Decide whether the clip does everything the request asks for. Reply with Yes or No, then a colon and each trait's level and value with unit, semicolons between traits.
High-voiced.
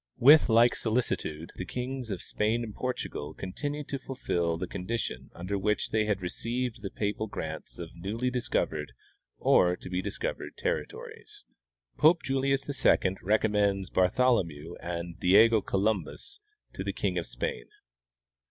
No: low, 105 Hz